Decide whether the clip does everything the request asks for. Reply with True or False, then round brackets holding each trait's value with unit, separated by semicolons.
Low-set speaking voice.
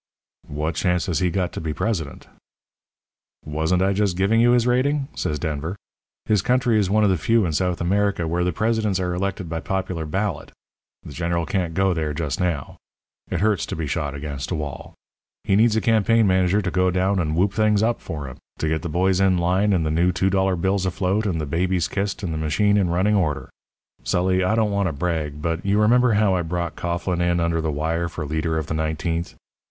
True (90 Hz)